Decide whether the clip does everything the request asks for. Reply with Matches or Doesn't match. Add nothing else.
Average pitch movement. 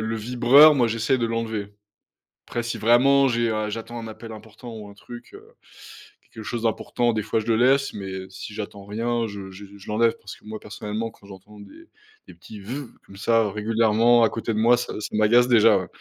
Doesn't match